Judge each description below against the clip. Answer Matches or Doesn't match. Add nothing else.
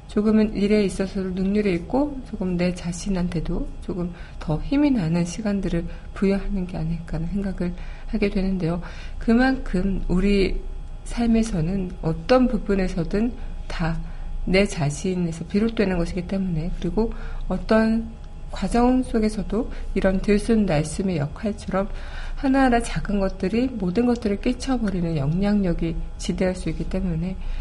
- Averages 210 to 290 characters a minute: Doesn't match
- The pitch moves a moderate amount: Matches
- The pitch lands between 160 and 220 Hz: Matches